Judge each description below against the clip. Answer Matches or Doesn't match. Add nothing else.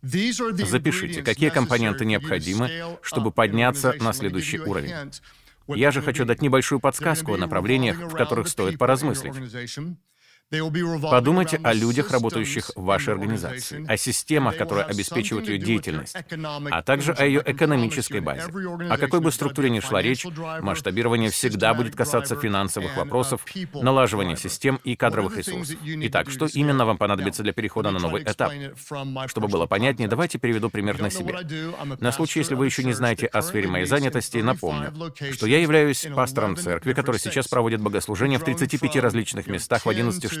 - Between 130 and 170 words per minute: Matches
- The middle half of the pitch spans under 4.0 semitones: Doesn't match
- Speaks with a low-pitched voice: Matches